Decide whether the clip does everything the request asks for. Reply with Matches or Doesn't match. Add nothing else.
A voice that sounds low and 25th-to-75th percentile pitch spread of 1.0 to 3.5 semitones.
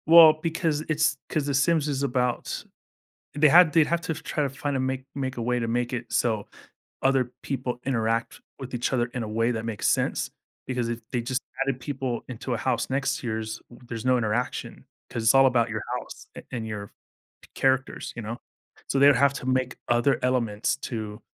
Matches